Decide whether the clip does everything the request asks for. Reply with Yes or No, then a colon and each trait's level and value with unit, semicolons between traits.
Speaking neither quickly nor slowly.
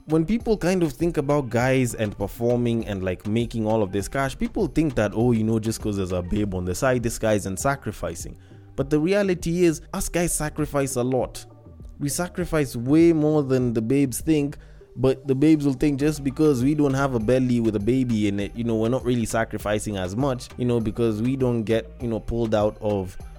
No: fast, 225 wpm